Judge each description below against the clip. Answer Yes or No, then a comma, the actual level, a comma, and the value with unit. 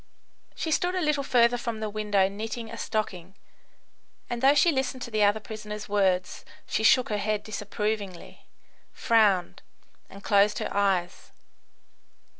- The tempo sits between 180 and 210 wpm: No, average, 145 wpm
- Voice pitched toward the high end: Yes, high, 215 Hz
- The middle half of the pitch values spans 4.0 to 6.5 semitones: No, average, 2.7 semitones